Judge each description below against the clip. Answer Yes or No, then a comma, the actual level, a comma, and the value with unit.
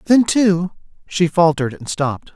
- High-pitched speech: No, medium, 170 Hz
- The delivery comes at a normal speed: Yes, average, 155 wpm